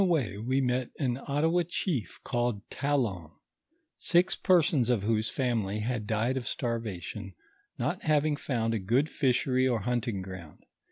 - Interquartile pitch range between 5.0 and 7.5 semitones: No, average, 4.4 semitones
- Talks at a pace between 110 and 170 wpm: Yes, average, 160 wpm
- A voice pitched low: Yes, low, 120 Hz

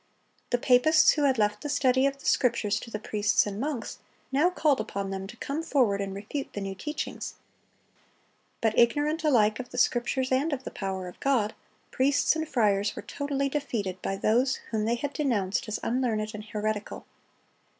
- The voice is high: Yes, high, 240 Hz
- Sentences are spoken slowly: No, average, 185 wpm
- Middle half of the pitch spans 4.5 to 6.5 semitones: Yes, average, 4.9 semitones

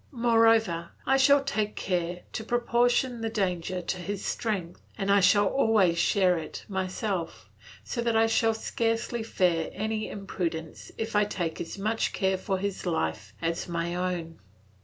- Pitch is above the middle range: Yes, high, 200 Hz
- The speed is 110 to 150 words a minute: No, average, 160 wpm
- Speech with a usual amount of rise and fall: Yes, average, 4.1 semitones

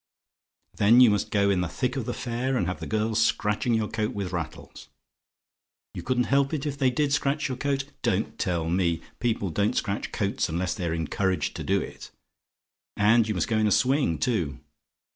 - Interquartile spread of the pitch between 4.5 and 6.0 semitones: Yes, average, 5.2 semitones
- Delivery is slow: No, average, 200 wpm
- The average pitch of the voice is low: Yes, low, 110 Hz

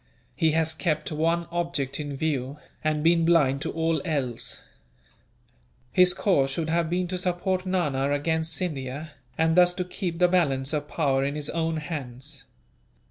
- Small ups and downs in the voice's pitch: No, average, 3.2 semitones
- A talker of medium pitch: Yes, medium, 160 Hz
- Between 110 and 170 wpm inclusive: Yes, average, 160 wpm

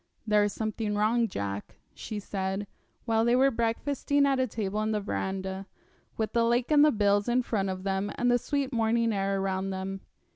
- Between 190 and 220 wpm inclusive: Yes, average, 195 wpm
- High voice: Yes, high, 215 Hz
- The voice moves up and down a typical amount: Yes, average, 3.5 semitones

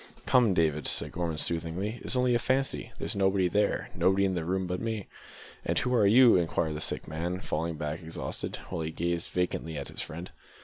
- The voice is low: Yes, very low, 90 Hz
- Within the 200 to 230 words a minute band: Yes, fast, 205 wpm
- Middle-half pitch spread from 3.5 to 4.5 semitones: Yes, average, 3.8 semitones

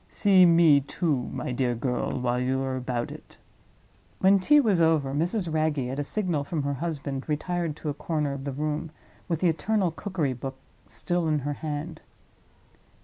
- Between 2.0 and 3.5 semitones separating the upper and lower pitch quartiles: No, average, 4.2 semitones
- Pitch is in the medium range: Yes, medium, 150 Hz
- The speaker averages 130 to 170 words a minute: No, average, 180 wpm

